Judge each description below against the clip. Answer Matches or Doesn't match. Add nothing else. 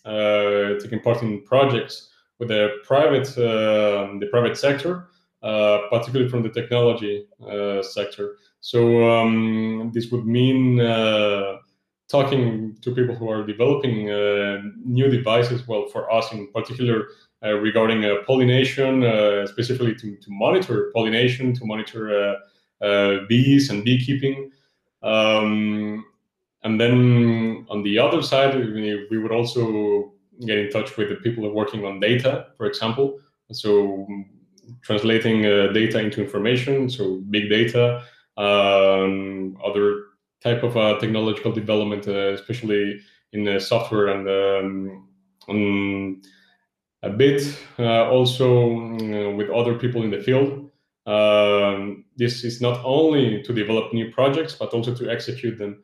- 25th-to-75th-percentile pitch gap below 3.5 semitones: Matches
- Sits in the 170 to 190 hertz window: Doesn't match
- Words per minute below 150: Matches